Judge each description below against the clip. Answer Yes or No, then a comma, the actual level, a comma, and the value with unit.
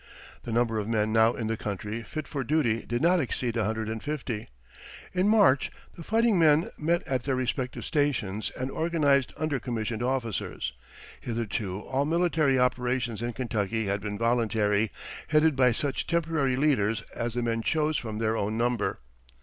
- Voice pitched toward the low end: Yes, low, 120 Hz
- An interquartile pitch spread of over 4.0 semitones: Yes, average, 4.7 semitones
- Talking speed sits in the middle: Yes, average, 170 wpm